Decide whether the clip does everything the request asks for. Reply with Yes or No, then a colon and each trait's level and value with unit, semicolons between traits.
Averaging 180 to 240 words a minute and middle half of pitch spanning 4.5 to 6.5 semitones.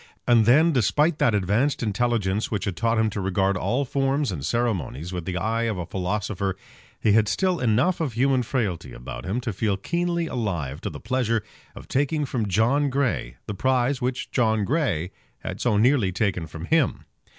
Yes: average, 185 wpm; wide, 5.4 semitones